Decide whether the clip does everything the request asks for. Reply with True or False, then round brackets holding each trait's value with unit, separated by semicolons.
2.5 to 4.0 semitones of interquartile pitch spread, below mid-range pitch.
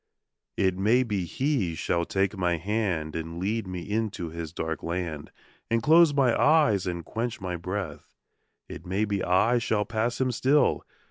False (4.9 semitones; 100 Hz)